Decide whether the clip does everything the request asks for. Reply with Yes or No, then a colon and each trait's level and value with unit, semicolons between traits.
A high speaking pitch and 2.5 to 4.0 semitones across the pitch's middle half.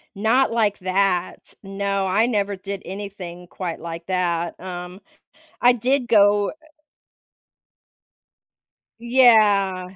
Yes: high, 195 Hz; average, 2.9 semitones